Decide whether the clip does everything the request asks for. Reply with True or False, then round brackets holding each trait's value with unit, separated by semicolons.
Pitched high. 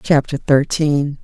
False (145 Hz)